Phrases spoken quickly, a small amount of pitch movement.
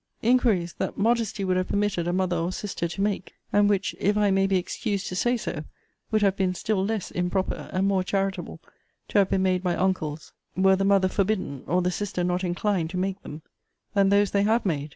Yes: fast, 215 wpm; narrow, 1.9 semitones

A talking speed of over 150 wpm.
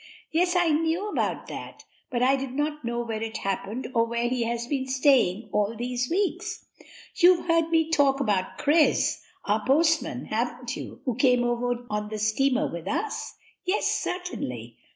Yes: average, 170 wpm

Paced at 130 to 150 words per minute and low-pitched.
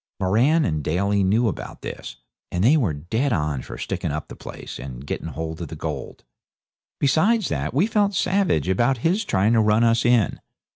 No: average, 190 wpm; low, 110 Hz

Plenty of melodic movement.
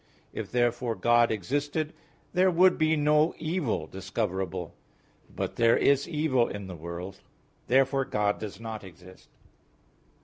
Yes: wide, 7.4 semitones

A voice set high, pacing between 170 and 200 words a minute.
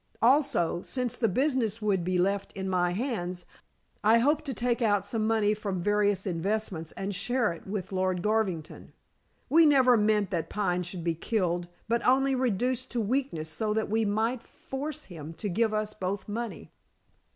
Yes: high, 210 Hz; average, 175 wpm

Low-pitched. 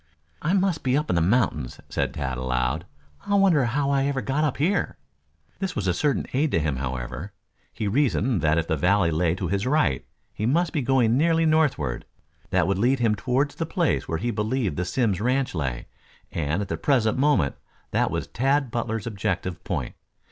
Yes: low, 110 Hz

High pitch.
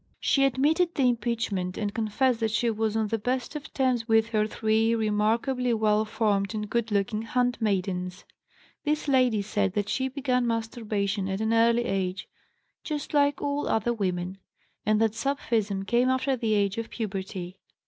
Yes: high, 225 Hz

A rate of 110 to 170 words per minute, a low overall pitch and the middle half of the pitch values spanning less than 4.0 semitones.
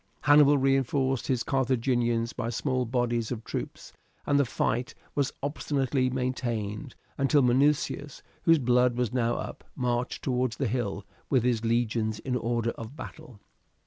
Yes: average, 145 wpm; low, 125 Hz; narrow, 2.5 semitones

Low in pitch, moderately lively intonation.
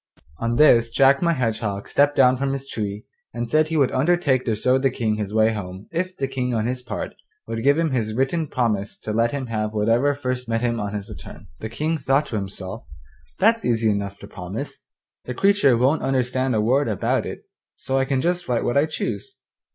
Yes: low, 125 Hz; average, 4.0 semitones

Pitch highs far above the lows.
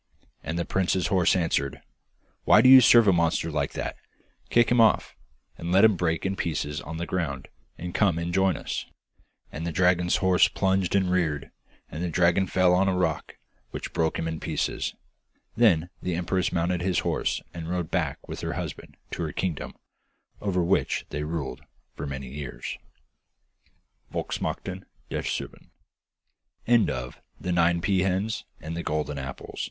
No: narrow, 2.6 semitones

